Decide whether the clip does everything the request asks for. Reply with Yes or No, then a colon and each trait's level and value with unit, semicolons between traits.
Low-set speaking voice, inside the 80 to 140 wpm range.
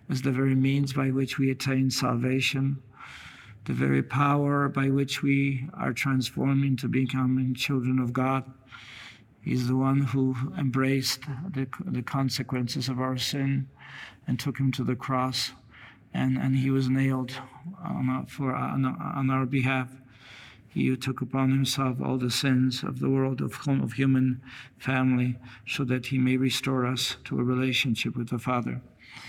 No: low, 130 Hz; average, 160 wpm